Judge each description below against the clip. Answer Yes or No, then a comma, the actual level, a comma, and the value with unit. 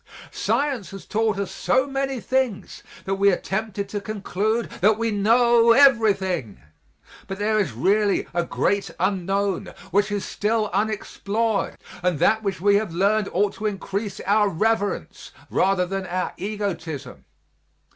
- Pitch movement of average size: No, narrow, 2.2 semitones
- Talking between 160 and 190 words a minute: No, average, 145 wpm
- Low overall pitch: No, high, 205 Hz